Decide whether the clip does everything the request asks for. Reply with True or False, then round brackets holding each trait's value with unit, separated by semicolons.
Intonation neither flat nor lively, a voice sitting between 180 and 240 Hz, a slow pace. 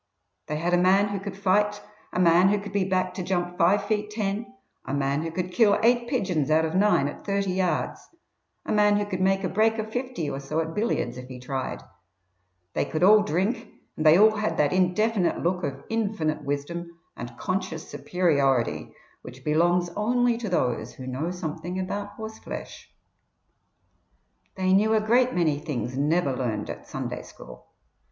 False (5.0 semitones; 185 Hz; 180 wpm)